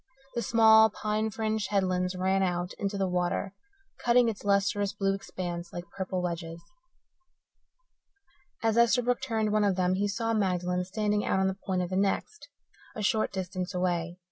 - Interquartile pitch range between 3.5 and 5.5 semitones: No, average, 3.0 semitones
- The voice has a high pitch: Yes, high, 195 Hz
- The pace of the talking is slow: No, average, 165 wpm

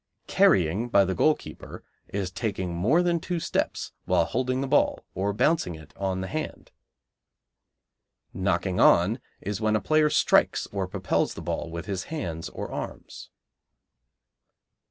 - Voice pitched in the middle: No, low, 100 Hz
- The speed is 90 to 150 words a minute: Yes, average, 145 wpm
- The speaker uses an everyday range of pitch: No, wide, 7.3 semitones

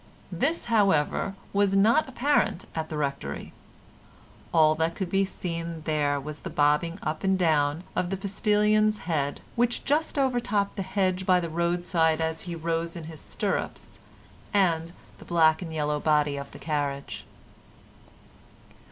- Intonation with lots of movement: No, average, 4.0 semitones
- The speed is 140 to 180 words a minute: Yes, average, 150 wpm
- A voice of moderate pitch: Yes, medium, 170 Hz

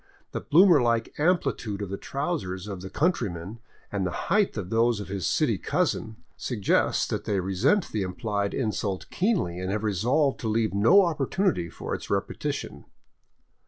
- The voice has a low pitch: Yes, low, 110 Hz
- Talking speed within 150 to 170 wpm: Yes, average, 165 wpm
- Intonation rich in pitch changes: Yes, wide, 6.7 semitones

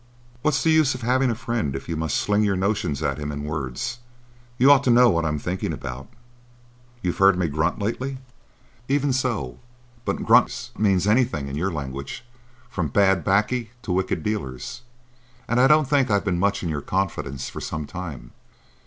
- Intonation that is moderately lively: No, wide, 8.1 semitones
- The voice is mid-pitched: No, very low, 95 Hz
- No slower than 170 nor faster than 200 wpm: Yes, average, 185 wpm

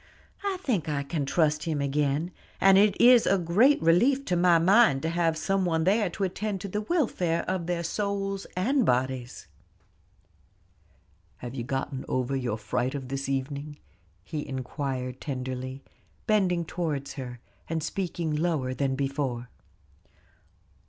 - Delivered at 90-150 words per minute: Yes, average, 145 wpm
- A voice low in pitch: No, medium, 160 Hz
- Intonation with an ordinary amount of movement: No, wide, 6.0 semitones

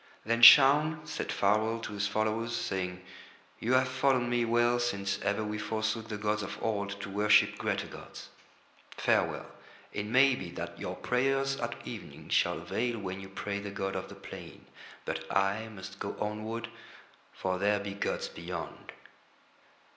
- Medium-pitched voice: No, low, 110 Hz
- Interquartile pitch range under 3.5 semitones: Yes, average, 3.0 semitones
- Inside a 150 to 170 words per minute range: Yes, average, 165 wpm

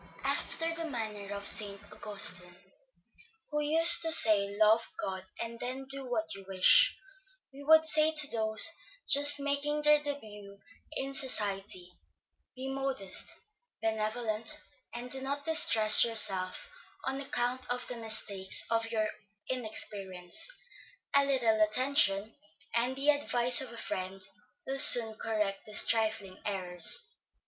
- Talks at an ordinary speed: No, slow, 130 wpm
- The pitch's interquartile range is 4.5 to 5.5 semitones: Yes, average, 5.0 semitones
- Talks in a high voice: Yes, high, 230 Hz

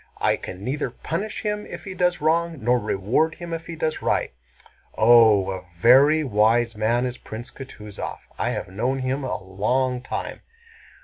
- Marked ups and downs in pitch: Yes, wide, 6.3 semitones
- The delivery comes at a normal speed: Yes, average, 170 wpm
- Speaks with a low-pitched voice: Yes, low, 125 Hz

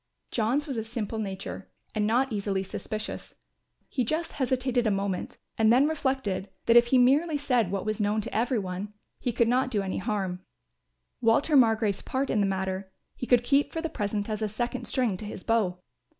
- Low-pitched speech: No, high, 225 Hz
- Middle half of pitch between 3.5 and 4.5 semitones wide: Yes, average, 4.1 semitones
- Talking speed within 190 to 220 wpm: Yes, average, 195 wpm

